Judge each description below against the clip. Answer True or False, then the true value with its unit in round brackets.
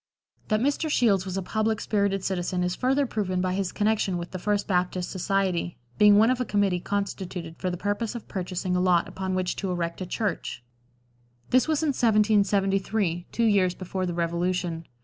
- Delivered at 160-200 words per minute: True (190 wpm)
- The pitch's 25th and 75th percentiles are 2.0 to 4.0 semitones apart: True (2.8 semitones)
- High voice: True (195 Hz)